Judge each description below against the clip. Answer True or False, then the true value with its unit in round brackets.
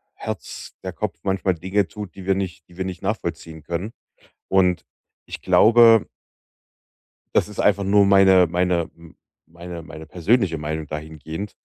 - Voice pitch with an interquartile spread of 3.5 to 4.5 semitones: False (2.9 semitones)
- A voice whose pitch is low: True (90 Hz)